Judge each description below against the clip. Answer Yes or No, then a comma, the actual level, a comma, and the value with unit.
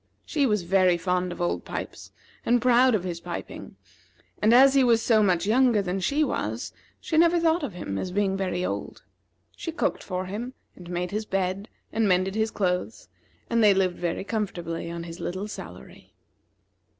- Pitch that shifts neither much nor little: Yes, average, 4.5 semitones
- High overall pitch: Yes, high, 195 Hz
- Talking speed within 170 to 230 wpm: Yes, average, 185 wpm